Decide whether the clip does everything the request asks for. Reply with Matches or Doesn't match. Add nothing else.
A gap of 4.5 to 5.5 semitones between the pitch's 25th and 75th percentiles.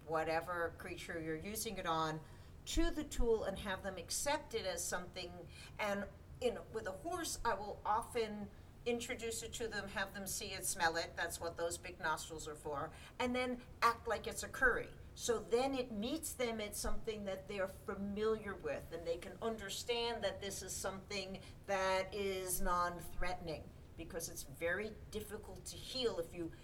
Matches